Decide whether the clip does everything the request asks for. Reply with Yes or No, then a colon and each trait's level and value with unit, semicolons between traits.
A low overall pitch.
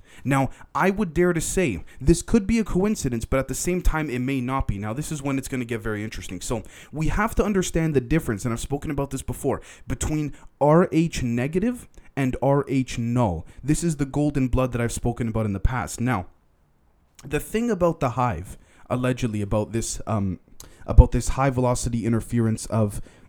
Yes: low, 130 Hz